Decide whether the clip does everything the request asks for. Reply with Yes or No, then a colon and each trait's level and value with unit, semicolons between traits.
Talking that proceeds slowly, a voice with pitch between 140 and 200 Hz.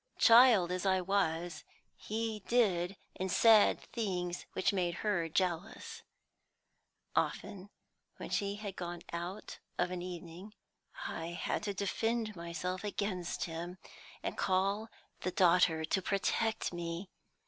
Yes: slow, 125 wpm; medium, 185 Hz